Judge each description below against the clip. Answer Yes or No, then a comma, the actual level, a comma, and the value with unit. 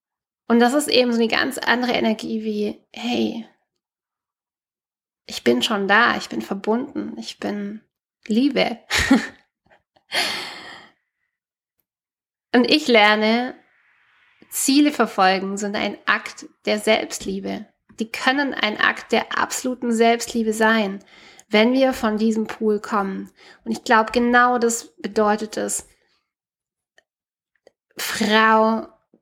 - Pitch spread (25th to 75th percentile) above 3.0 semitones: No, narrow, 2.6 semitones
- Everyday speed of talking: No, slow, 110 wpm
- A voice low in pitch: No, high, 220 Hz